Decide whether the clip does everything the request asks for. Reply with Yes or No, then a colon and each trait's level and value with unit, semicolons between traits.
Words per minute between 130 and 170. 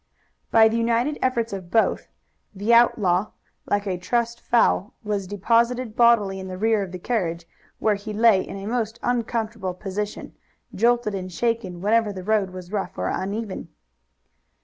Yes: average, 160 wpm